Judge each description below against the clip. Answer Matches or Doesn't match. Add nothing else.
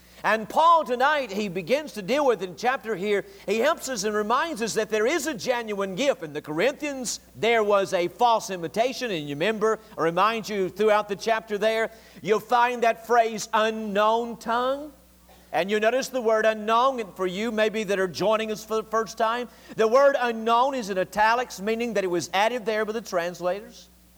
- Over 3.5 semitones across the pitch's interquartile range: Doesn't match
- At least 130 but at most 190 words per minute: Doesn't match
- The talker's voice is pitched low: Doesn't match